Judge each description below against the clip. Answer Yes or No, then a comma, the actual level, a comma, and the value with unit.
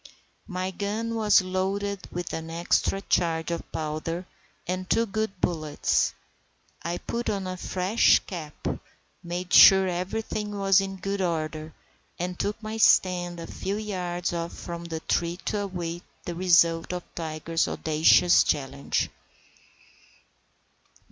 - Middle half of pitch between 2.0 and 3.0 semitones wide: Yes, narrow, 2.6 semitones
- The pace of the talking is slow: Yes, slow, 130 wpm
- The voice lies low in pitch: No, medium, 180 Hz